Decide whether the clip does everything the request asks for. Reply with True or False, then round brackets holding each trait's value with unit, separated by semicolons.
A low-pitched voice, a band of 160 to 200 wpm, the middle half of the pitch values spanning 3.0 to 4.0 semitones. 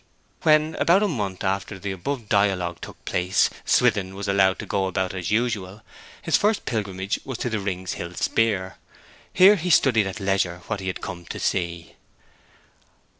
True (100 Hz; 175 wpm; 3.4 semitones)